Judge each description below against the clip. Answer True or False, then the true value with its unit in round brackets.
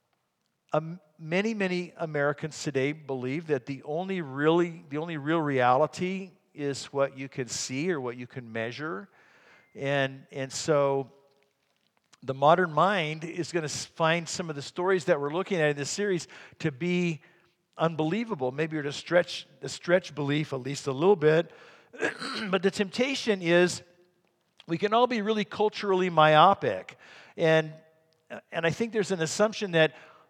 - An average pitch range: True (4.3 semitones)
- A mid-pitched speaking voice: True (160 Hz)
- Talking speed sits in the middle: True (155 wpm)